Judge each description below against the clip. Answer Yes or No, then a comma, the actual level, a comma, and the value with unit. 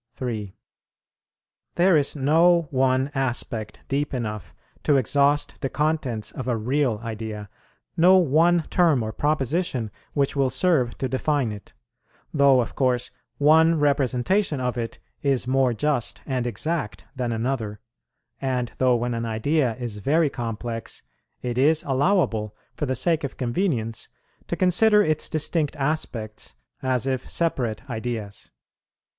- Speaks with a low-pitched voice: Yes, low, 130 Hz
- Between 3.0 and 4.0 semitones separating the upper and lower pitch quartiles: No, average, 4.5 semitones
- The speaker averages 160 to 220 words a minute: No, slow, 135 wpm